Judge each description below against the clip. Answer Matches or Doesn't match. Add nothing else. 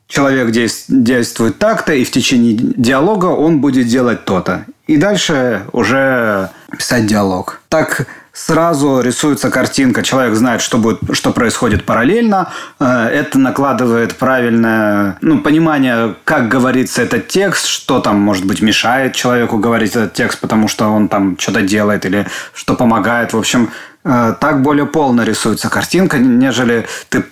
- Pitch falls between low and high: Doesn't match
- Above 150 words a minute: Doesn't match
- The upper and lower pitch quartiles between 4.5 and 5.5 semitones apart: Matches